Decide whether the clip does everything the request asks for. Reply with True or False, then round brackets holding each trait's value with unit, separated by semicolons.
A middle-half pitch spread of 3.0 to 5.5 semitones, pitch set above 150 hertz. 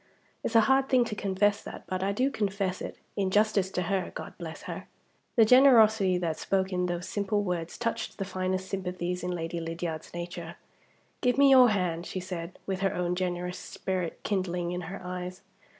False (2.6 semitones; 185 Hz)